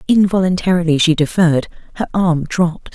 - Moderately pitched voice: Yes, medium, 175 Hz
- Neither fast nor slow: No, slow, 120 wpm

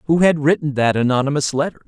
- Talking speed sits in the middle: Yes, average, 190 wpm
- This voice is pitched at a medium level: Yes, medium, 145 Hz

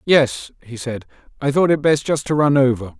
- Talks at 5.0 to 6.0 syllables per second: Yes, 5.1 syllables/s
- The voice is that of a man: Yes, male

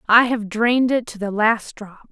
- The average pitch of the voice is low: No, high, 225 Hz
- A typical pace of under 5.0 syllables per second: Yes, 4.7 syllables/s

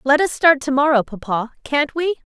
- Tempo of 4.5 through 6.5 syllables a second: Yes, 5.1 syllables/s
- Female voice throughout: Yes, female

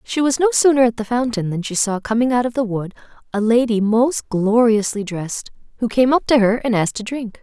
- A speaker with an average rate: No, fast, 235 wpm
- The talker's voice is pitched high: Yes, high, 230 Hz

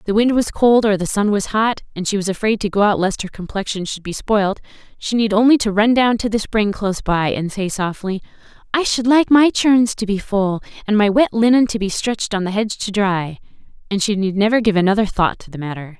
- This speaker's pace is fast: Yes, fast, 250 wpm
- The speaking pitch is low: No, high, 205 Hz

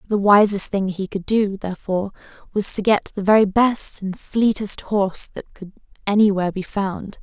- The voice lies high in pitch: Yes, high, 200 Hz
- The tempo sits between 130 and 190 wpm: Yes, average, 175 wpm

